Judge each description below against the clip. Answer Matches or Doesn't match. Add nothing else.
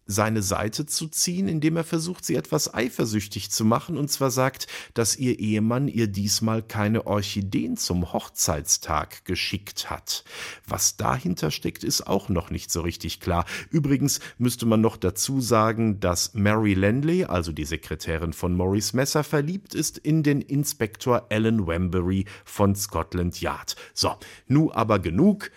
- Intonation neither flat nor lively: Doesn't match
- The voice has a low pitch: Matches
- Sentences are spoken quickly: Doesn't match